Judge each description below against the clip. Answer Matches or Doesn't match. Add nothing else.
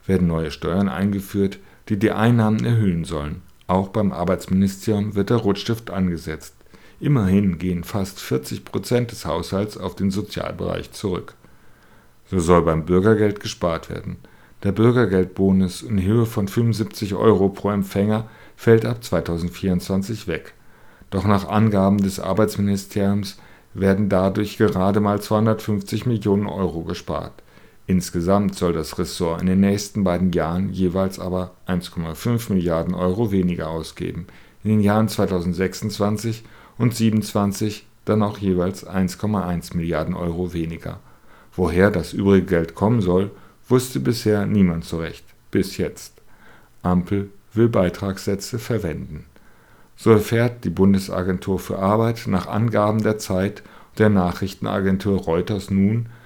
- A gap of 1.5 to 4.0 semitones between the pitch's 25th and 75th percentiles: Matches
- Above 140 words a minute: Doesn't match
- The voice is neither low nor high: Doesn't match